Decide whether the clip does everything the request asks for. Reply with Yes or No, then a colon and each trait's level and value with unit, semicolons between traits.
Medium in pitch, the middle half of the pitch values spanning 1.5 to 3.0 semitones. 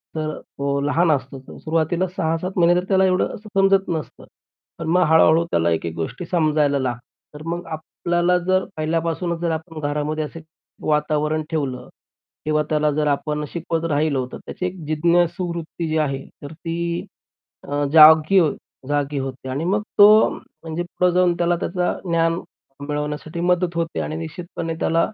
Yes: medium, 160 Hz; narrow, 2.6 semitones